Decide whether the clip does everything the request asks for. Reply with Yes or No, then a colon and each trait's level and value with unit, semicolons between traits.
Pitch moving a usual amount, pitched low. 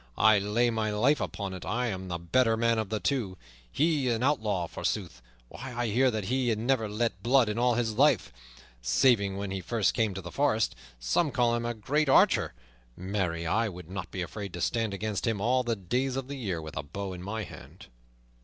Yes: average, 4.2 semitones; low, 110 Hz